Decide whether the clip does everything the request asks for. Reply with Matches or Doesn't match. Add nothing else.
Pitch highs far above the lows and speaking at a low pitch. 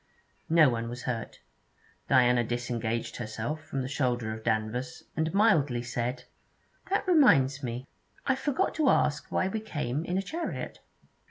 Matches